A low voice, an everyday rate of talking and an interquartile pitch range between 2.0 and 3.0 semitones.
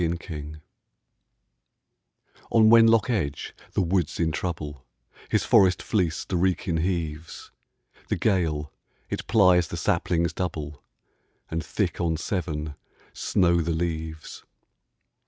No: very low, 85 Hz; slow, 110 wpm; average, 2.7 semitones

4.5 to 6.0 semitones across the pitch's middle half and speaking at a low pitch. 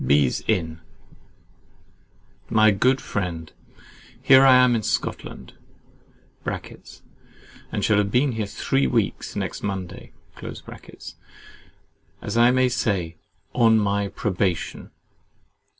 Yes: average, 5.1 semitones; low, 105 Hz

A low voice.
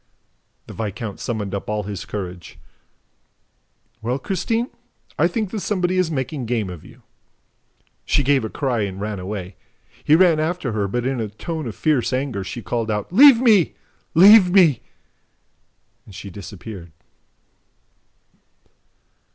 Yes: low, 120 Hz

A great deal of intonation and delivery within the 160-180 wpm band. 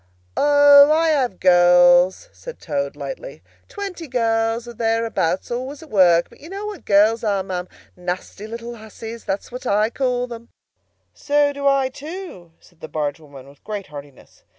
Yes: wide, 7.9 semitones; average, 165 wpm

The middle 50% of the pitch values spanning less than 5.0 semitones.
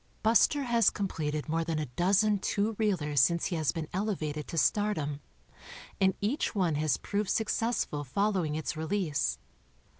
No: average, 5.3 semitones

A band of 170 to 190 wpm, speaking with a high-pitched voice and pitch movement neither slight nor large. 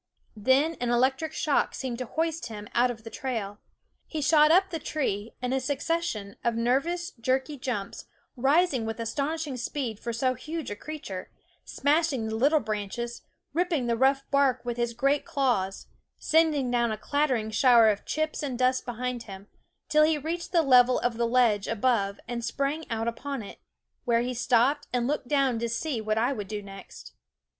Yes: average, 180 wpm; very high, 250 Hz; average, 4.1 semitones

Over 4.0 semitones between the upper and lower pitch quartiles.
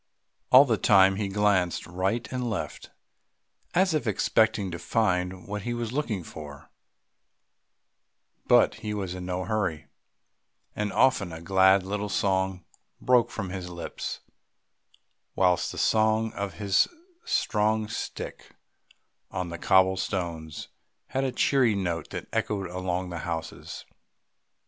No: average, 3.3 semitones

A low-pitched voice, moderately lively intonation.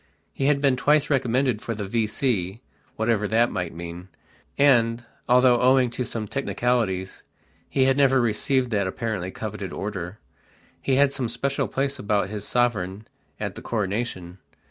Yes: low, 115 Hz; average, 4.5 semitones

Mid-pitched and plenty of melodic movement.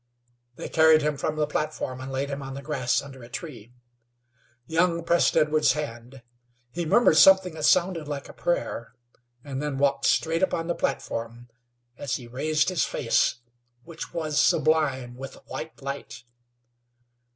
No: medium, 150 Hz; average, 3.3 semitones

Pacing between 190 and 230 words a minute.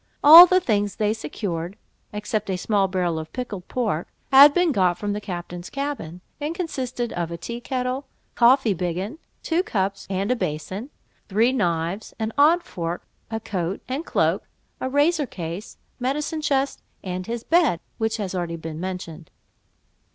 No: average, 160 wpm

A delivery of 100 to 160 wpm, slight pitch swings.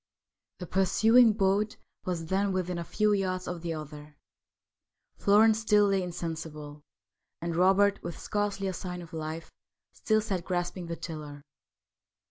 No: average, 140 wpm; average, 3.5 semitones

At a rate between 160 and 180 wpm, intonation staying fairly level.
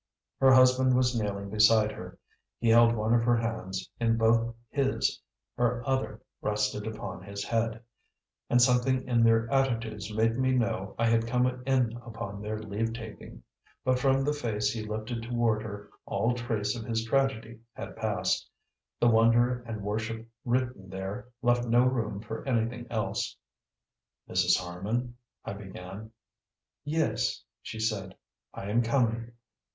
No: average, 150 wpm; narrow, 2.2 semitones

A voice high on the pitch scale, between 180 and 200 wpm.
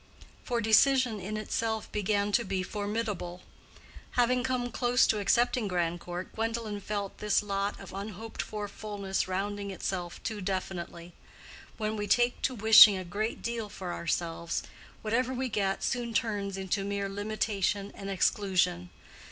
No: high, 205 Hz; average, 145 wpm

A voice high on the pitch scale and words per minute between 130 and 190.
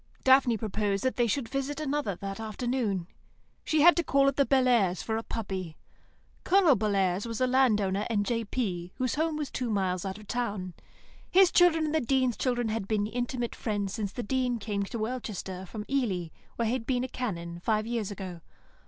No: high, 225 Hz; average, 200 wpm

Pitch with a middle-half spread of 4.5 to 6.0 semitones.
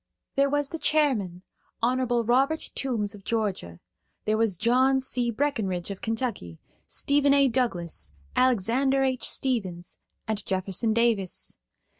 Yes: average, 5.1 semitones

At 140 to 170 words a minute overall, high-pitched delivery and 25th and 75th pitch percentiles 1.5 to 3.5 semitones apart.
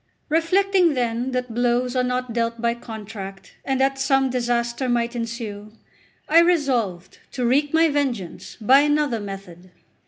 Yes: average, 145 wpm; high, 245 Hz; average, 3.1 semitones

